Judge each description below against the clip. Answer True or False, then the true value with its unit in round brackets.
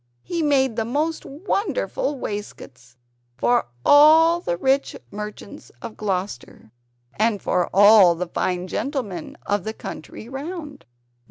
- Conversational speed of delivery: False (120 wpm)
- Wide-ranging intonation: True (7.5 semitones)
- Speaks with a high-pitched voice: True (225 Hz)